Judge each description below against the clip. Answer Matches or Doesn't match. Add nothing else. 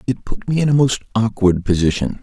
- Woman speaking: Doesn't match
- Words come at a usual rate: Doesn't match